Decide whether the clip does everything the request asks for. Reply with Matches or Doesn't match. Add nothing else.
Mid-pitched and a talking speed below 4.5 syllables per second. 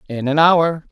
Matches